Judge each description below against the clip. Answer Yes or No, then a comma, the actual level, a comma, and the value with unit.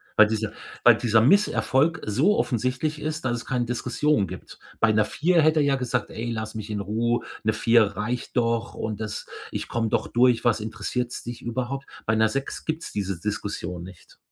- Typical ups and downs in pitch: Yes, average, 3.2 semitones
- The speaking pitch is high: No, low, 120 Hz